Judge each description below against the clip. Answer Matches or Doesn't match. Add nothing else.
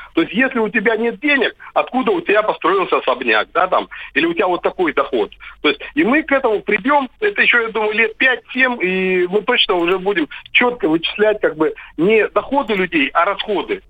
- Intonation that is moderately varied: Doesn't match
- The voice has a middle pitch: Doesn't match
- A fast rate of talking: Matches